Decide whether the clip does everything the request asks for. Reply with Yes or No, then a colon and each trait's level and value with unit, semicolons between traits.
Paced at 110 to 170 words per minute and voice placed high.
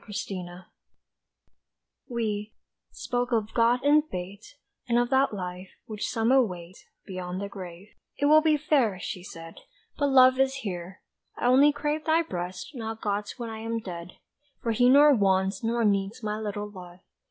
Yes: average, 165 wpm; high, 220 Hz